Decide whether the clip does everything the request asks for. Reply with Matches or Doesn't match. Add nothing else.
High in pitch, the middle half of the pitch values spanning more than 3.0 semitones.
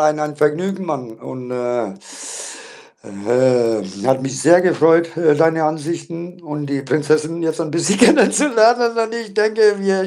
Doesn't match